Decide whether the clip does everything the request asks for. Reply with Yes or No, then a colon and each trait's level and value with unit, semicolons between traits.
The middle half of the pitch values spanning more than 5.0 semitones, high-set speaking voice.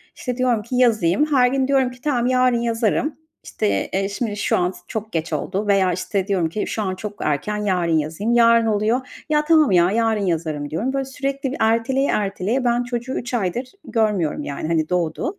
Yes: wide, 5.4 semitones; high, 220 Hz